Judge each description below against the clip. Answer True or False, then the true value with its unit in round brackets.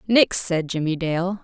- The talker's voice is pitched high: False (180 Hz)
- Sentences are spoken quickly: False (165 wpm)